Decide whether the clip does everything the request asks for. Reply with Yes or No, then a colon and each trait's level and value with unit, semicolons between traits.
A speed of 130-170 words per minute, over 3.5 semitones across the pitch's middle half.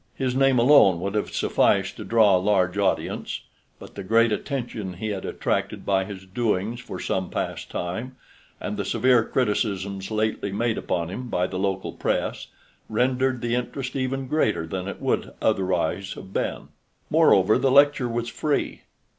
Yes: average, 165 wpm; average, 4.6 semitones